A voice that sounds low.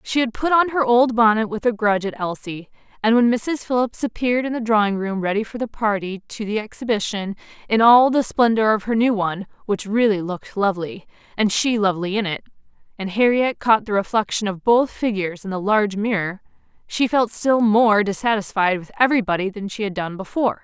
No: high, 215 Hz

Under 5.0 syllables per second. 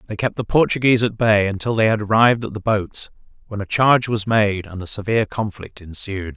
No: 5.8 syllables/s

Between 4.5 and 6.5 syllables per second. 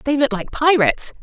Yes: 5.4 syllables/s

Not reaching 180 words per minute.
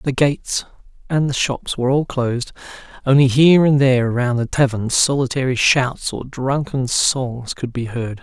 Yes: average, 160 wpm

